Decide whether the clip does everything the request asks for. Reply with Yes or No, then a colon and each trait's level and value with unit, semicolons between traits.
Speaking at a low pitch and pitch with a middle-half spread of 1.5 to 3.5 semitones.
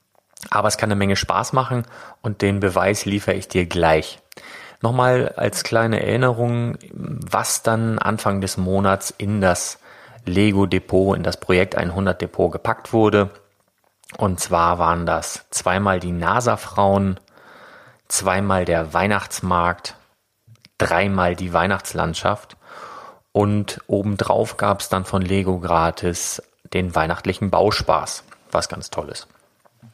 Yes: low, 100 Hz; narrow, 2.6 semitones